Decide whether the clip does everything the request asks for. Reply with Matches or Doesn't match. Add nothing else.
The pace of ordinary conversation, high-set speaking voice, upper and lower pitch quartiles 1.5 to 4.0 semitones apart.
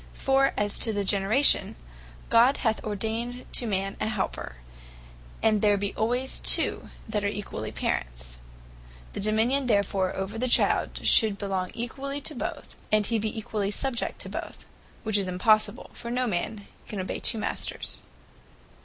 Matches